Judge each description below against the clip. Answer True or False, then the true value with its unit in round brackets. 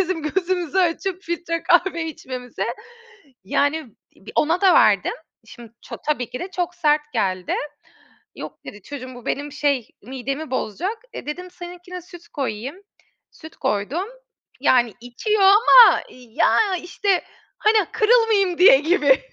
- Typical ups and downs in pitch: False (6.0 semitones)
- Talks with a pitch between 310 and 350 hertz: True (325 Hz)